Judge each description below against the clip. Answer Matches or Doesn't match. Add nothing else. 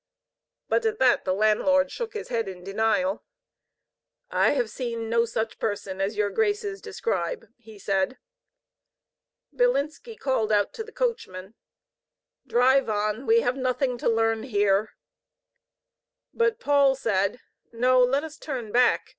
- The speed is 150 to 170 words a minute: Doesn't match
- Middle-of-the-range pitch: Doesn't match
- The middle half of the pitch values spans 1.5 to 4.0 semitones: Doesn't match